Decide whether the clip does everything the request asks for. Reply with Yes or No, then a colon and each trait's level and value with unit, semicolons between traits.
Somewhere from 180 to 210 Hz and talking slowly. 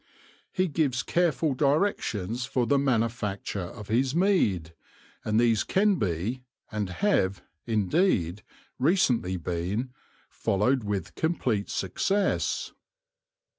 No: low, 120 Hz; slow, 100 wpm